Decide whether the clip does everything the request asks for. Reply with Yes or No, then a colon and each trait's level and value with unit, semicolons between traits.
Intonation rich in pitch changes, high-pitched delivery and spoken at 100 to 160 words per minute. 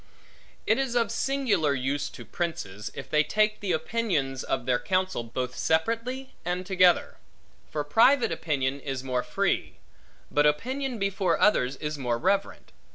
No: wide, 8.0 semitones; medium, 165 Hz; average, 150 wpm